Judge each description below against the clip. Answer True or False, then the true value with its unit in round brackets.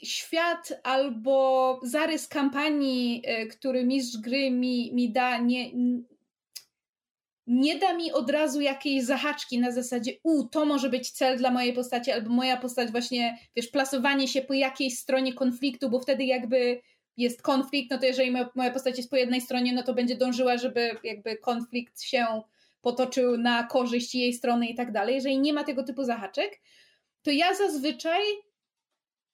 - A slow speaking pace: False (160 wpm)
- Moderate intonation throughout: False (2.0 semitones)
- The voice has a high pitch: True (255 Hz)